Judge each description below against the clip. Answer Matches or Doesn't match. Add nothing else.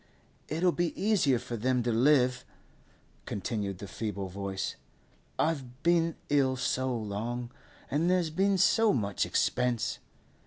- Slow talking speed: Matches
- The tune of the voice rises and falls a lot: Matches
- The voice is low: Matches